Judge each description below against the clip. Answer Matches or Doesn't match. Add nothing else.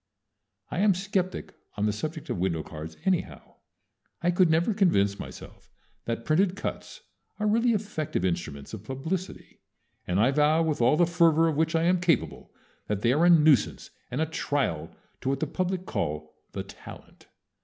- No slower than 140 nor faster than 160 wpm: Doesn't match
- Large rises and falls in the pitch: Matches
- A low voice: Doesn't match